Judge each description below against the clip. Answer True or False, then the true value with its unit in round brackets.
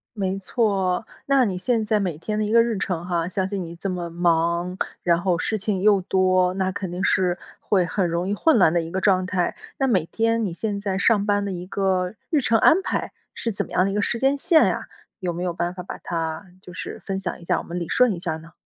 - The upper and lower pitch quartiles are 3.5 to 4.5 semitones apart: False (3.0 semitones)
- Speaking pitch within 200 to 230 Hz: False (190 Hz)